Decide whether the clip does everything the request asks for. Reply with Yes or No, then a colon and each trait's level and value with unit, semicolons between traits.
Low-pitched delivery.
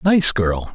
Yes: low, 130 Hz